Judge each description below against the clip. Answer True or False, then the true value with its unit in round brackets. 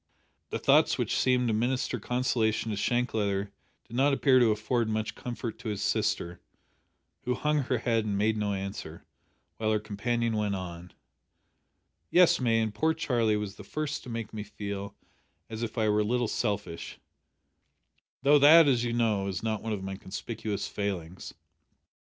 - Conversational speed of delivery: True (175 wpm)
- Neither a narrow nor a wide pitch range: True (3.1 semitones)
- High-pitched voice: False (110 Hz)